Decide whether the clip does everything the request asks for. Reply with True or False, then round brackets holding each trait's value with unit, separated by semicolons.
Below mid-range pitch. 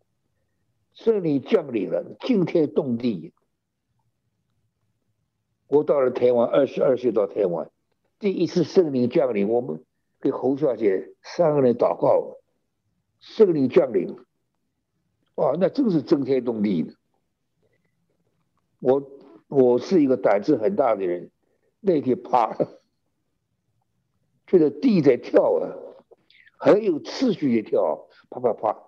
False (170 Hz)